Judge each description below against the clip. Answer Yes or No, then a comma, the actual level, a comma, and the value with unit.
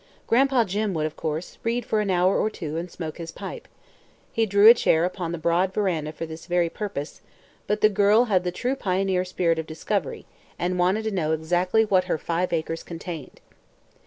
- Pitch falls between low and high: Yes, medium, 180 Hz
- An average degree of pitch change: Yes, average, 3.9 semitones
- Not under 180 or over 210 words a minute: Yes, average, 200 wpm